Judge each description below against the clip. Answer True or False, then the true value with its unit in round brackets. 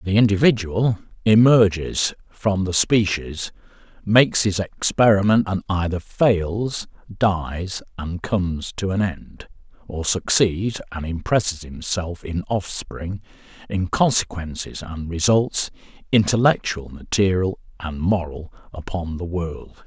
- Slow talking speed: True (110 wpm)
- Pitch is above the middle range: False (95 Hz)